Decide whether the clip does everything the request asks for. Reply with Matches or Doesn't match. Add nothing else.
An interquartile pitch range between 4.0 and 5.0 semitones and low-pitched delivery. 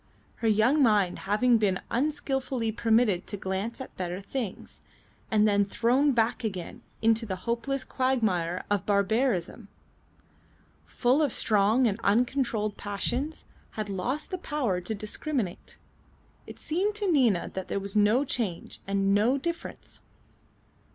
Doesn't match